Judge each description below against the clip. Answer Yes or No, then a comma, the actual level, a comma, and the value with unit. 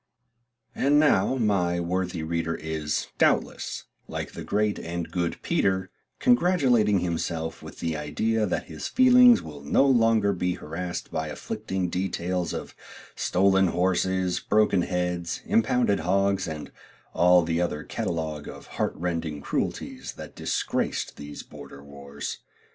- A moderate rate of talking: No, slow, 130 wpm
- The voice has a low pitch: Yes, very low, 90 Hz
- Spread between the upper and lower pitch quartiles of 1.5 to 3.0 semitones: No, average, 3.7 semitones